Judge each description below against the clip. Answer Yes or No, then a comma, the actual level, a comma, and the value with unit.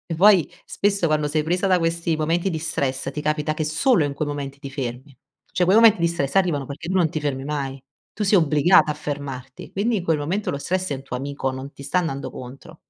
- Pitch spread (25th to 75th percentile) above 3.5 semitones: Yes, average, 4.1 semitones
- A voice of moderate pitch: Yes, medium, 155 Hz